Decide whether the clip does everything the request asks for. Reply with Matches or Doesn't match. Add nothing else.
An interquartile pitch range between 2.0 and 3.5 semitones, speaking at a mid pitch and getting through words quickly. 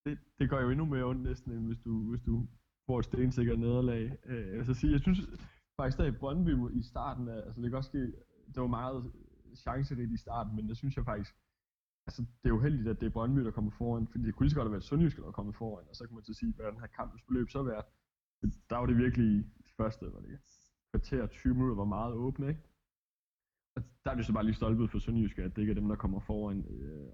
Doesn't match